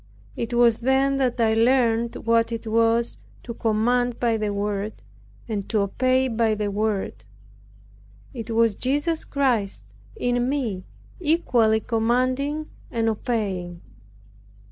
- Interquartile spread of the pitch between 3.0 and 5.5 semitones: No, narrow, 2.6 semitones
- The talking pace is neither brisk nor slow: No, slow, 120 wpm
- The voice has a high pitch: Yes, high, 230 Hz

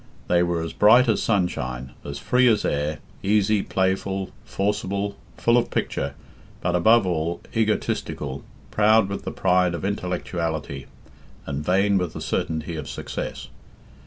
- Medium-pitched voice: No, very low, 90 Hz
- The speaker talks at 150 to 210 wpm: No, average, 140 wpm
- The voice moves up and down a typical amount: Yes, average, 4.2 semitones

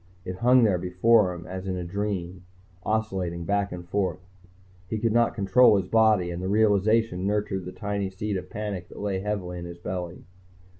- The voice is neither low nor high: No, very low, 95 Hz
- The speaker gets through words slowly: No, average, 190 wpm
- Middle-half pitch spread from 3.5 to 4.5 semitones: No, average, 2.7 semitones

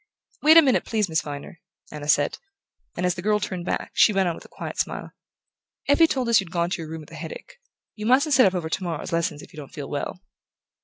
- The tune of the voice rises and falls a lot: Yes, wide, 6.0 semitones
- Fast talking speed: Yes, fast, 245 wpm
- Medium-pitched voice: Yes, medium, 180 Hz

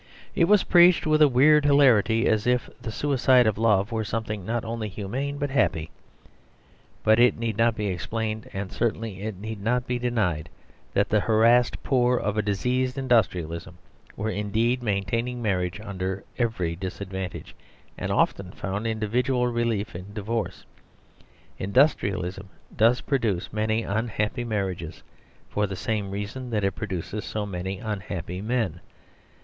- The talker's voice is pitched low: Yes, low, 110 Hz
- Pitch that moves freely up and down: No, average, 3.7 semitones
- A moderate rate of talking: Yes, average, 145 wpm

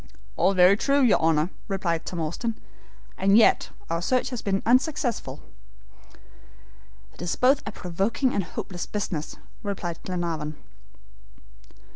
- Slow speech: Yes, slow, 125 wpm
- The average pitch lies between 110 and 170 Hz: No, high, 195 Hz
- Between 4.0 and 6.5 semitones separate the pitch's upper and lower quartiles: Yes, average, 5.3 semitones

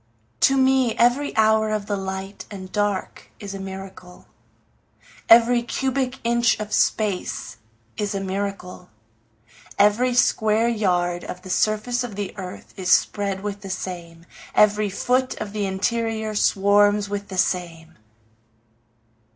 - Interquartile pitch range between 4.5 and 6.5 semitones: No, average, 2.8 semitones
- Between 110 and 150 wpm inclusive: Yes, slow, 135 wpm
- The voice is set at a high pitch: Yes, high, 205 Hz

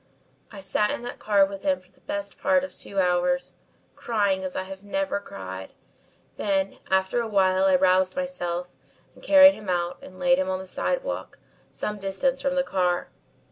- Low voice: No, high, 195 Hz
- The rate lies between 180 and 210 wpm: Yes, average, 185 wpm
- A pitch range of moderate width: No, wide, 6.3 semitones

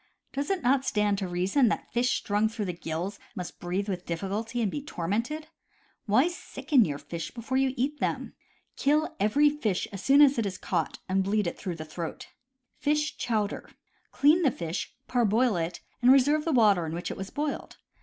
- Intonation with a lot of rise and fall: Yes, wide, 6.8 semitones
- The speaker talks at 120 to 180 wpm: No, average, 195 wpm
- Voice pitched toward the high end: Yes, high, 215 Hz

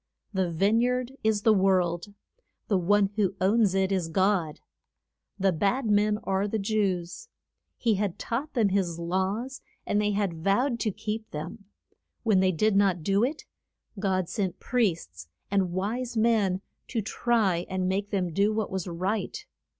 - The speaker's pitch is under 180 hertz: No, high, 200 Hz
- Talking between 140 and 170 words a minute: Yes, average, 160 wpm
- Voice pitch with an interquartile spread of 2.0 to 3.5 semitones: Yes, average, 2.7 semitones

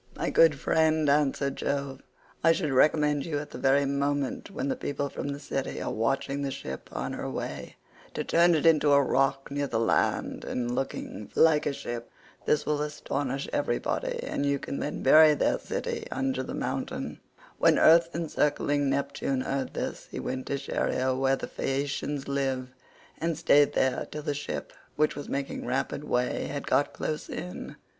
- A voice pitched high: No, medium, 140 Hz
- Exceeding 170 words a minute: Yes, average, 180 wpm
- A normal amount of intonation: No, narrow, 1.8 semitones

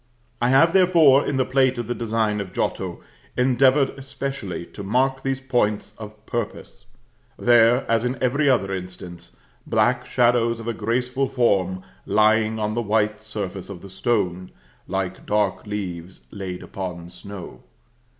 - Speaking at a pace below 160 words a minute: Yes, average, 150 wpm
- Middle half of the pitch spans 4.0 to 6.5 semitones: Yes, average, 4.5 semitones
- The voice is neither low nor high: No, low, 110 Hz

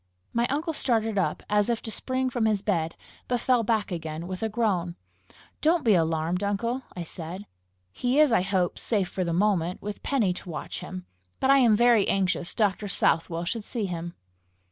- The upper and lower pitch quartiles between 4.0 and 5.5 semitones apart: Yes, average, 4.9 semitones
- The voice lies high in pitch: Yes, high, 205 Hz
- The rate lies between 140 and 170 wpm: No, average, 190 wpm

